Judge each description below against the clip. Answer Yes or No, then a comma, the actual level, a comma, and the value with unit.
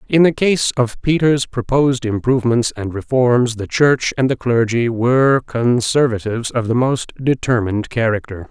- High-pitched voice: No, low, 125 Hz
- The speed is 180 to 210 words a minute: No, average, 150 wpm